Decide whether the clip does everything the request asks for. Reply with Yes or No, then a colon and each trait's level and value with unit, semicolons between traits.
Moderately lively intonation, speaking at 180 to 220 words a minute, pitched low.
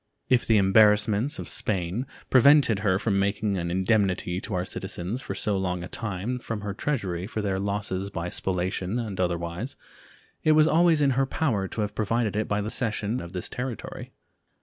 Yes: average, 3.9 semitones; average, 185 wpm; low, 105 Hz